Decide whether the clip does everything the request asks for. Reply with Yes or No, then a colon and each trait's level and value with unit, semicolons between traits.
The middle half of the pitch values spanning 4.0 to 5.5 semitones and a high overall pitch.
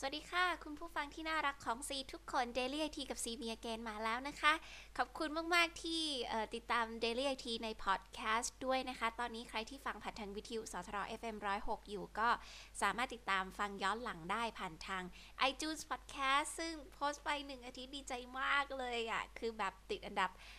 Yes: average, 4.5 semitones; high, 240 Hz